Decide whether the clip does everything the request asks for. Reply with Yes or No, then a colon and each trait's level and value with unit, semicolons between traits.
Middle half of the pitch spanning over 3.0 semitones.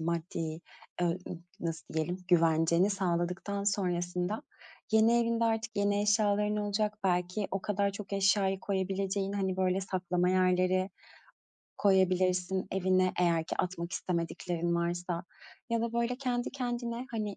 No: average, 2.7 semitones